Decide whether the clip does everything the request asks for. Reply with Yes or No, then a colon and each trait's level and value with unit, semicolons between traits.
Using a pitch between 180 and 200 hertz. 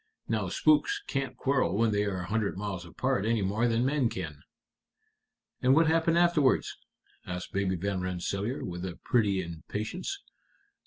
No: low, 105 Hz